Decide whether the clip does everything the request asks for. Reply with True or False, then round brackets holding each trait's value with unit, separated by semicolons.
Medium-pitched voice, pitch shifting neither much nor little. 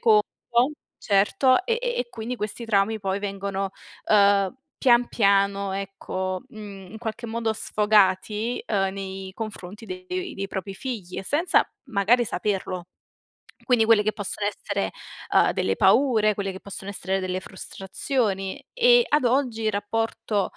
False (210 Hz; 3.1 semitones)